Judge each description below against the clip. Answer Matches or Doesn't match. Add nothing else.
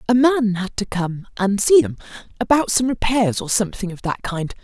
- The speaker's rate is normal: Matches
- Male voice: Doesn't match